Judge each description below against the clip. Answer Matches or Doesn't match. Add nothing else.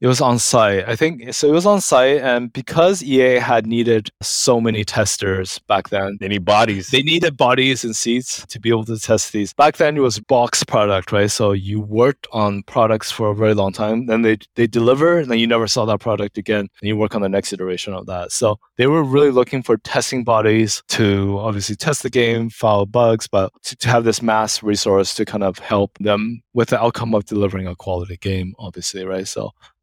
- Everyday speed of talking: Doesn't match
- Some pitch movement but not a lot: Matches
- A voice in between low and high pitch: Doesn't match